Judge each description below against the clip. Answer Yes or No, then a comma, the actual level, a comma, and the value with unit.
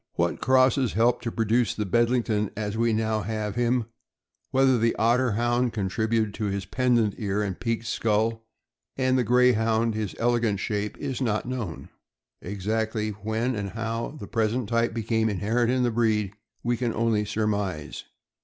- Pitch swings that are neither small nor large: No, narrow, 2.2 semitones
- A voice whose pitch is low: Yes, low, 115 Hz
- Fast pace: No, average, 165 wpm